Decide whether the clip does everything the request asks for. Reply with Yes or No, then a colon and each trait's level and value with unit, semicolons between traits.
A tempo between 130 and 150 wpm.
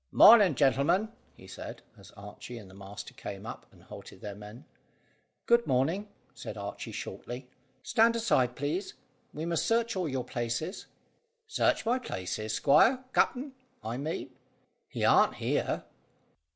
Yes: average, 140 wpm